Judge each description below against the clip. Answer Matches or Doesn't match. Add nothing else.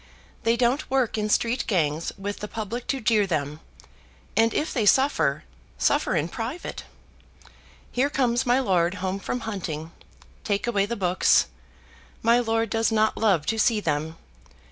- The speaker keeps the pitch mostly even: Doesn't match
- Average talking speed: Matches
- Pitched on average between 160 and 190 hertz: Doesn't match